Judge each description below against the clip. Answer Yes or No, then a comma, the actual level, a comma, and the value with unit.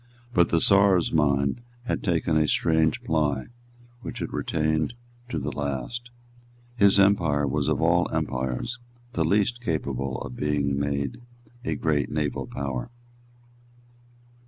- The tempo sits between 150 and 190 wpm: No, slow, 135 wpm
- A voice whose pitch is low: Yes, very low, 75 Hz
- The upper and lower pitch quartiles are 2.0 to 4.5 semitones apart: No, average, 5.2 semitones